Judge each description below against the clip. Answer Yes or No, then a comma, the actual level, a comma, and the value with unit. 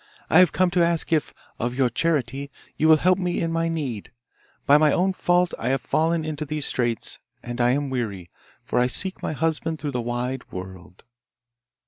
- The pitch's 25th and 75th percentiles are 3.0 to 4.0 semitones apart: No, average, 5.1 semitones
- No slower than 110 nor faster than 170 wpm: No, average, 195 wpm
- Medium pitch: Yes, medium, 145 Hz